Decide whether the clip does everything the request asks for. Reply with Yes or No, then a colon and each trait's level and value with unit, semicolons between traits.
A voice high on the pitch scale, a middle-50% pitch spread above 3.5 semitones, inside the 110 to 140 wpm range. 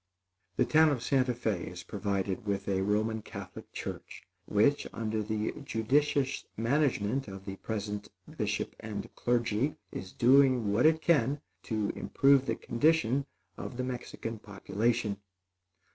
No: low, 115 Hz; average, 4.6 semitones; slow, 135 wpm